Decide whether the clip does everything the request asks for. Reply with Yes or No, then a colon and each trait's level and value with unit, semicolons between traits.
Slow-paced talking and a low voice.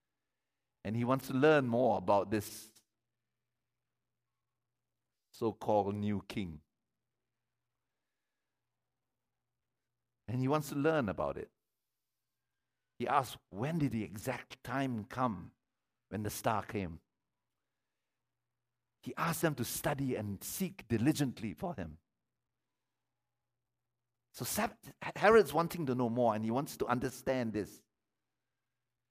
Yes: slow, 110 wpm; low, 120 Hz